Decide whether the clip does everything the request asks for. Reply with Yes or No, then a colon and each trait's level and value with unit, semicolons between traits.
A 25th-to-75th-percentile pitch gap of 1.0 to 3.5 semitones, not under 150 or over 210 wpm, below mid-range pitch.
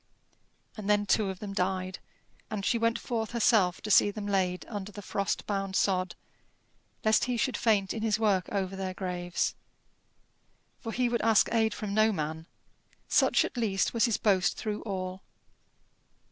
No: average, 2.7 semitones; average, 170 wpm; high, 205 Hz